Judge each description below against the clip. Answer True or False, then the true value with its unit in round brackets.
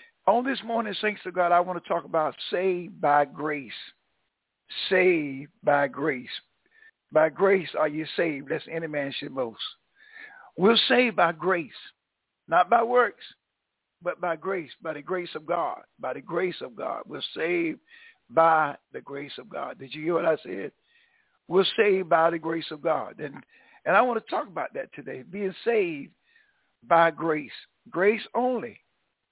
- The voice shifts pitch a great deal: True (6.9 semitones)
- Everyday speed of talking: True (170 wpm)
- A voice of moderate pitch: True (180 Hz)